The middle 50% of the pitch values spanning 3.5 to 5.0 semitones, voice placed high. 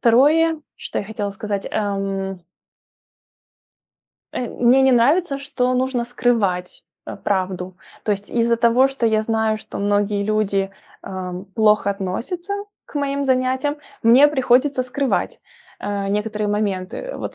Yes: average, 4.5 semitones; high, 225 Hz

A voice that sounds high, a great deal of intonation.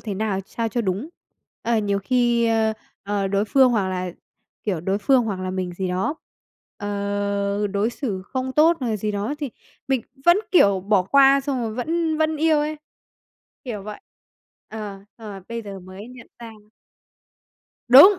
No: high, 215 Hz; average, 4.5 semitones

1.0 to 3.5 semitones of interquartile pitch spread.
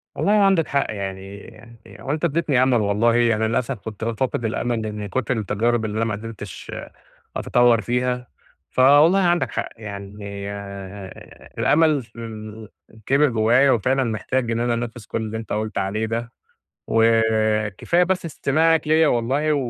No: average, 3.9 semitones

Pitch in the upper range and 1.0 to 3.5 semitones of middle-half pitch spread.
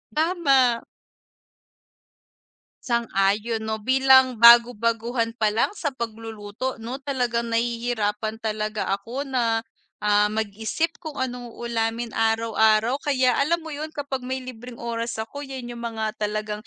Yes: high, 235 Hz; average, 2.9 semitones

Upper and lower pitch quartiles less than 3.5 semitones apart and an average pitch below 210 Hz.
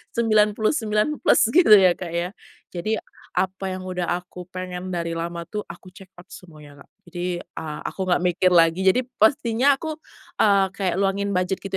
Yes: average, 3.1 semitones; medium, 185 Hz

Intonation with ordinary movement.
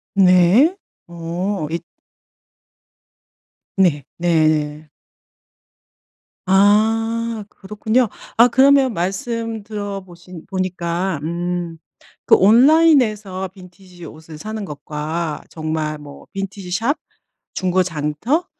Yes: average, 4.3 semitones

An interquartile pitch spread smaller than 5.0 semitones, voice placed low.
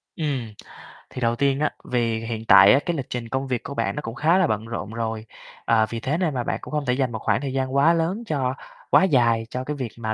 Yes: average, 3.9 semitones; low, 130 Hz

